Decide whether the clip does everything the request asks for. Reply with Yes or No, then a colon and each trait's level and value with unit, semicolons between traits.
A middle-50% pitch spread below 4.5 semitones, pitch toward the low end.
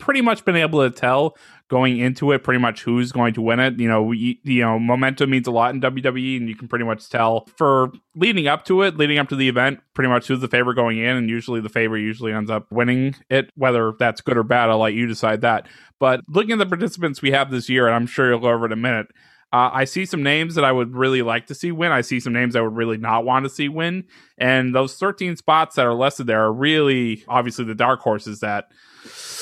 Yes: average, 3.2 semitones; low, 125 Hz